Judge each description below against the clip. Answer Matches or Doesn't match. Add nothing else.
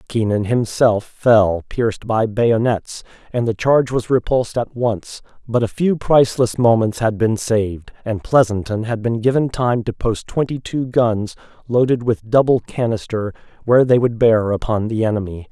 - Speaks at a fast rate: Doesn't match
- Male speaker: Matches